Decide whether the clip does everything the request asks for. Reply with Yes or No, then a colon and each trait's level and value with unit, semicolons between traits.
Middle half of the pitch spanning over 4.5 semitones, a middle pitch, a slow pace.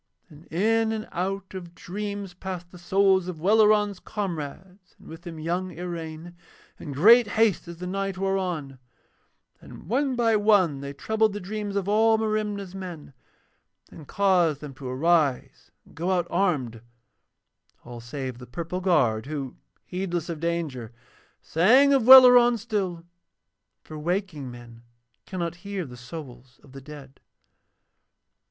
No: average, 5.0 semitones; medium, 180 Hz; average, 145 wpm